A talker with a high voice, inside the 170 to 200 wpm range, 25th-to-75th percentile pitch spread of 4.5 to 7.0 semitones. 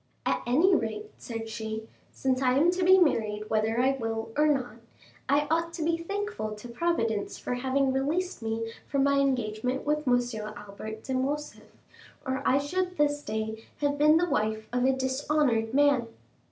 Yes: very high, 265 Hz; average, 175 wpm; average, 5.1 semitones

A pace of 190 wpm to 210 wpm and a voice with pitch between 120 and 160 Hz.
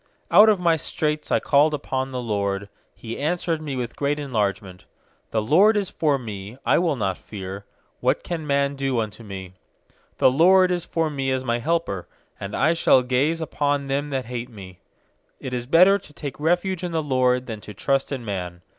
Yes: average, 200 wpm; low, 135 Hz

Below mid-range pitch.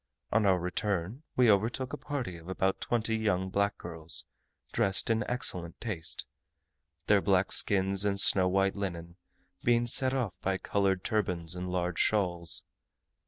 Yes: very low, 95 Hz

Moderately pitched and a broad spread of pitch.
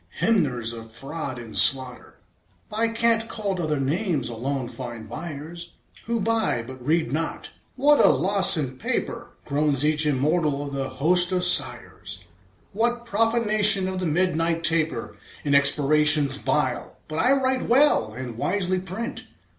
Yes: medium, 160 Hz; wide, 6.7 semitones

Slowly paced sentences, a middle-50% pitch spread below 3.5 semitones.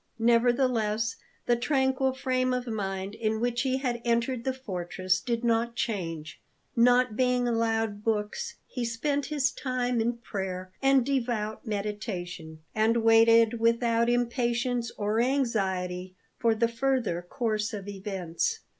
Yes: slow, 130 wpm; average, 2.9 semitones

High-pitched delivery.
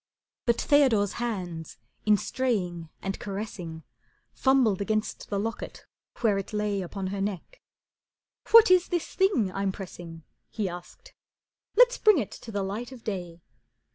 Yes: high, 205 Hz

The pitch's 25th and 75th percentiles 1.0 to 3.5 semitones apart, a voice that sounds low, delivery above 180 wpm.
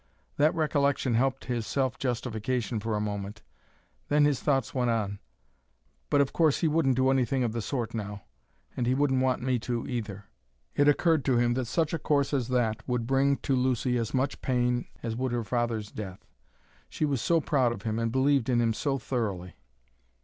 Yes: average, 3.2 semitones; low, 125 Hz; average, 195 wpm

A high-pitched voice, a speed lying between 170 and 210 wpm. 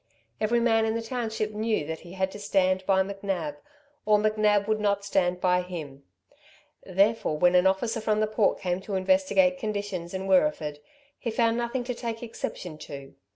Yes: high, 205 Hz; average, 180 wpm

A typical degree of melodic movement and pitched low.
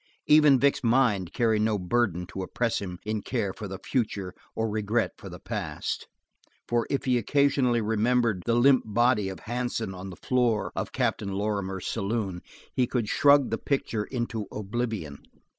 Yes: average, 3.7 semitones; low, 110 Hz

